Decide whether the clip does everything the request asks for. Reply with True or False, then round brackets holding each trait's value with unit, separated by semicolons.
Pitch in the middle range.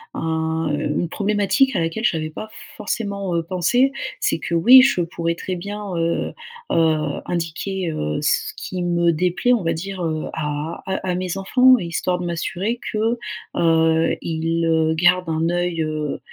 True (170 Hz)